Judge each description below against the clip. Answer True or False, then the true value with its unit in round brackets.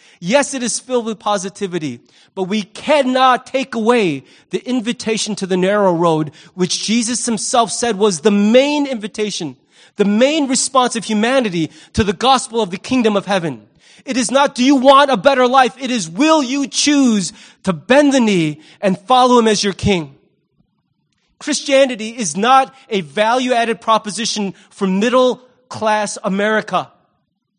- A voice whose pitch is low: False (220 Hz)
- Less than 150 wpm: False (160 wpm)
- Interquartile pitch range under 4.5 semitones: False (4.8 semitones)